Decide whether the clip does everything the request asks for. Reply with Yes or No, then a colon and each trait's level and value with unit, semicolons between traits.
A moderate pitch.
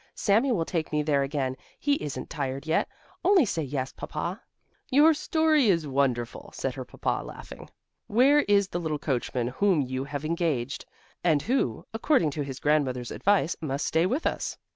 Yes: medium, 155 Hz